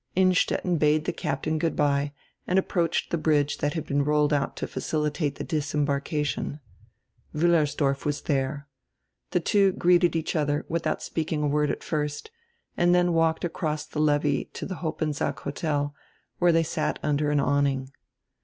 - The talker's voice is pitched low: No, medium, 150 Hz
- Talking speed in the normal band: Yes, average, 160 wpm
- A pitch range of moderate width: No, narrow, 2.2 semitones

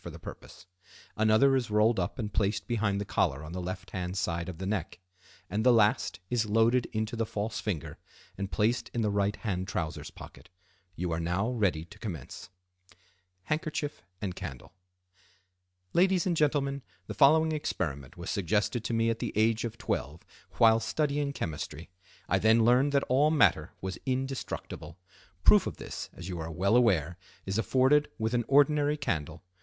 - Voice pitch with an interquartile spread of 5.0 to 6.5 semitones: Yes, average, 5.3 semitones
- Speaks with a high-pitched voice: No, low, 105 Hz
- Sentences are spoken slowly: No, average, 170 wpm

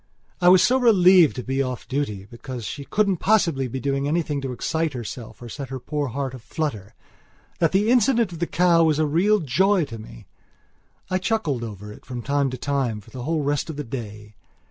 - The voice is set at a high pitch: No, medium, 140 Hz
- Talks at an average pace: No, fast, 210 wpm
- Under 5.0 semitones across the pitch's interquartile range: No, wide, 5.6 semitones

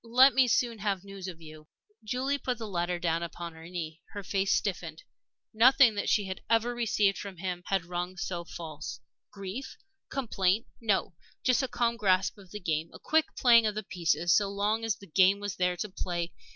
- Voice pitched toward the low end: No, high, 195 Hz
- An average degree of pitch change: Yes, average, 4.4 semitones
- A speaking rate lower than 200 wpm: No, fast, 205 wpm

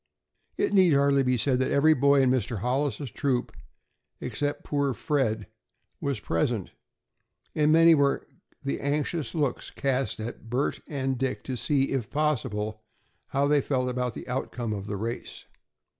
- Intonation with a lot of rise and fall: No, average, 2.8 semitones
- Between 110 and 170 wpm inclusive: Yes, average, 155 wpm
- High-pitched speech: No, low, 135 Hz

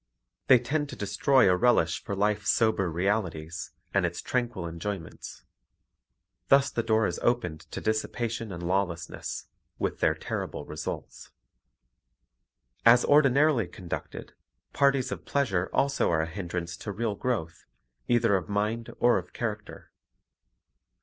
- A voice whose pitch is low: Yes, low, 105 Hz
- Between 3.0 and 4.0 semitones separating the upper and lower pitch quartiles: No, wide, 5.4 semitones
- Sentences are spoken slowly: Yes, slow, 130 wpm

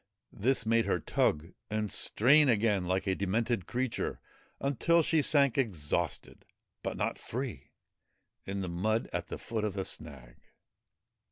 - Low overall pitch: Yes, low, 110 Hz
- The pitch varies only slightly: No, average, 5.3 semitones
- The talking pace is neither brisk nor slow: Yes, average, 145 wpm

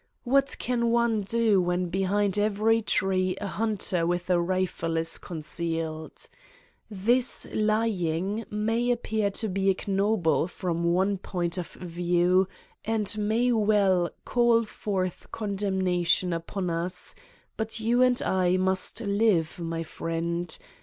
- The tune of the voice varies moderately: Yes, average, 3.7 semitones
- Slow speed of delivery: Yes, slow, 125 wpm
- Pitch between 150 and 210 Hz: Yes, high, 190 Hz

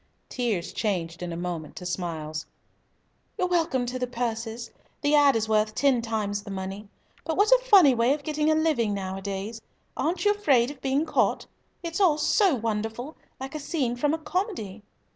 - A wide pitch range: Yes, wide, 6.9 semitones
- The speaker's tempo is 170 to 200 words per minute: Yes, average, 180 wpm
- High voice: Yes, high, 245 Hz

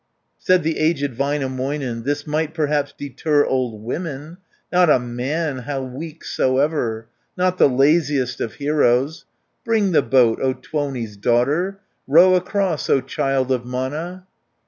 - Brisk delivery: No, slow, 135 wpm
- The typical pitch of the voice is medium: Yes, medium, 145 Hz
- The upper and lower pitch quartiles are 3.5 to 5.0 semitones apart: Yes, average, 3.8 semitones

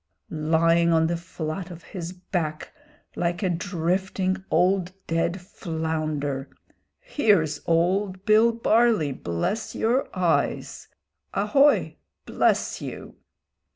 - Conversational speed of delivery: No, slow, 100 wpm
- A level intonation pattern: No, average, 3.4 semitones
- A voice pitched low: No, medium, 175 Hz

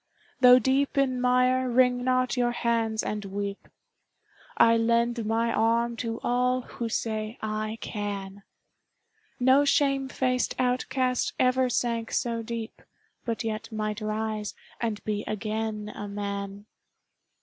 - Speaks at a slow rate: Yes, slow, 125 wpm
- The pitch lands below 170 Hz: No, high, 230 Hz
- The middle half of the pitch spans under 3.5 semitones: Yes, average, 2.8 semitones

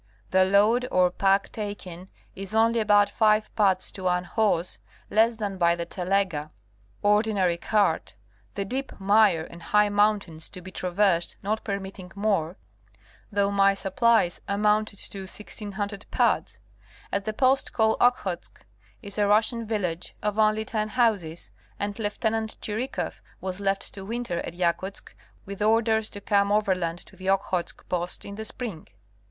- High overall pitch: Yes, high, 200 Hz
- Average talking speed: Yes, average, 150 wpm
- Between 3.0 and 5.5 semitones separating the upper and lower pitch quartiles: No, narrow, 2.5 semitones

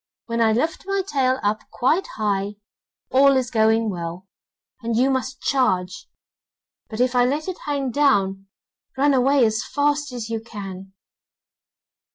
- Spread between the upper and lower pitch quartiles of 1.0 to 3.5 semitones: No, average, 4.4 semitones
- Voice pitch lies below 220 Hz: No, high, 245 Hz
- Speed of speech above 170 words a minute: No, average, 150 wpm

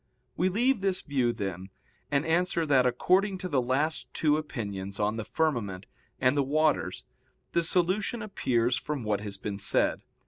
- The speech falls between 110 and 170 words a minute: Yes, average, 165 wpm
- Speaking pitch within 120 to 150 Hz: Yes, medium, 140 Hz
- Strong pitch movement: Yes, wide, 7.4 semitones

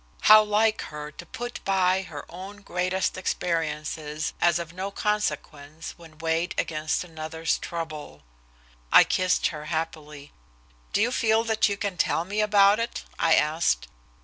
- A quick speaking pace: No, average, 150 wpm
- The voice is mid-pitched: Yes, medium, 170 Hz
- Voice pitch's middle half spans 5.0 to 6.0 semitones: No, average, 4.4 semitones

